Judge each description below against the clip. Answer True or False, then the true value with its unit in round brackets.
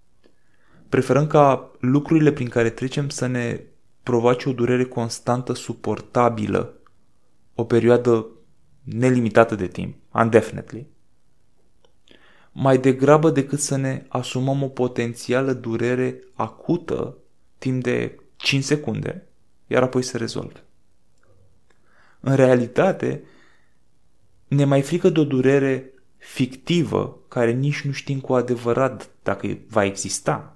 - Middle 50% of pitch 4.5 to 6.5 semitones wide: False (2.7 semitones)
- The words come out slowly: True (110 wpm)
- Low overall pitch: True (125 Hz)